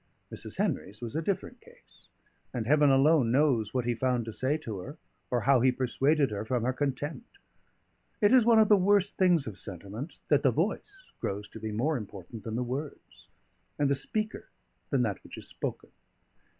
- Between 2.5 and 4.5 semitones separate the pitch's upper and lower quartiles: No, wide, 5.6 semitones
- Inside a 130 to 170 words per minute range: No, average, 190 wpm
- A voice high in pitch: No, low, 135 Hz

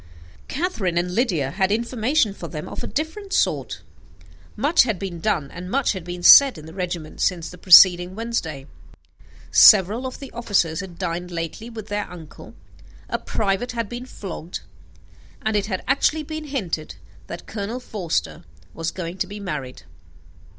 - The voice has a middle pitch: No, high, 195 Hz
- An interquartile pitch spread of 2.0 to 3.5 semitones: No, average, 5.3 semitones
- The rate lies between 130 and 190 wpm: Yes, average, 165 wpm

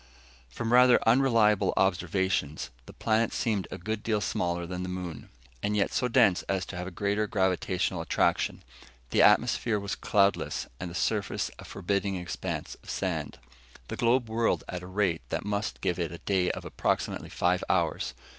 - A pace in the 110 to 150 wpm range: No, average, 175 wpm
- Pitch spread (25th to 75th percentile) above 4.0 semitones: No, average, 3.2 semitones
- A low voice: Yes, low, 100 Hz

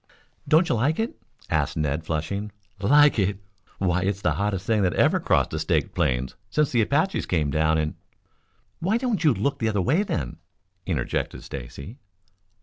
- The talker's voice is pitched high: No, low, 100 Hz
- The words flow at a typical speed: Yes, average, 175 wpm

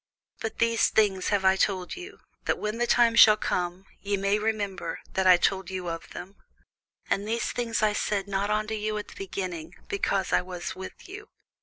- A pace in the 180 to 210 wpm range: Yes, average, 195 wpm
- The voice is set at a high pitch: Yes, high, 200 Hz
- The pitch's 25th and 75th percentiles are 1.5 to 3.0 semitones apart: Yes, narrow, 2.6 semitones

